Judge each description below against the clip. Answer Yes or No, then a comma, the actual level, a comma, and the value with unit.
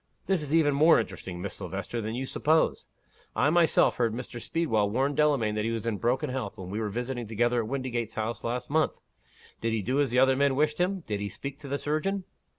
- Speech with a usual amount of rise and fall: Yes, average, 4.6 semitones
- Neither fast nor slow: No, fast, 230 wpm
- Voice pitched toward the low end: Yes, low, 125 Hz